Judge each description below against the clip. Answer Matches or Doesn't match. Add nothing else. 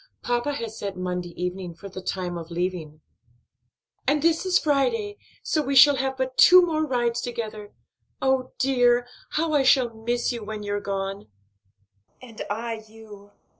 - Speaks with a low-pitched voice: Doesn't match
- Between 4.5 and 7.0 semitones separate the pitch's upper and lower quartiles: Matches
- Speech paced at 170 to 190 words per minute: Doesn't match